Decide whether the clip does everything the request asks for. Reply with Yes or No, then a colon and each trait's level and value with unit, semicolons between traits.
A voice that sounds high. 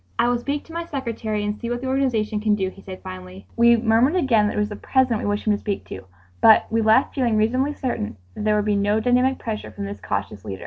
Yes: high, 220 Hz